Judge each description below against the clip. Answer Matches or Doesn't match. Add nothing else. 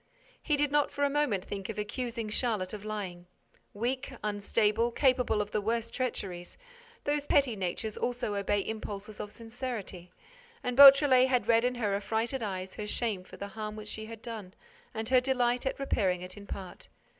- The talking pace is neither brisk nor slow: Matches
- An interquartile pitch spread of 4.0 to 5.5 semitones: Doesn't match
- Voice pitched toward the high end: Matches